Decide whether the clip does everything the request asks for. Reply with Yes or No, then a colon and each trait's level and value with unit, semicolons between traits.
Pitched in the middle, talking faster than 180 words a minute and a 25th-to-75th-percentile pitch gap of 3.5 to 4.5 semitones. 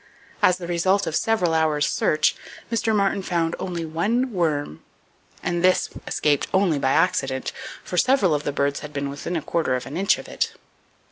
Yes: medium, 170 Hz; average, 190 wpm; average, 4.2 semitones